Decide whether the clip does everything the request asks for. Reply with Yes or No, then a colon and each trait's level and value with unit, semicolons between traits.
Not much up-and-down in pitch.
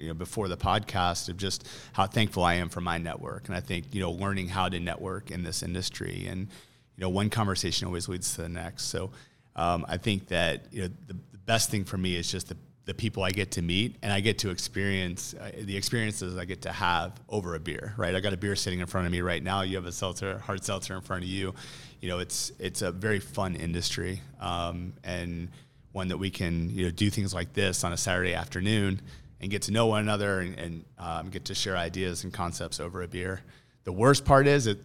Yes: narrow, 2.3 semitones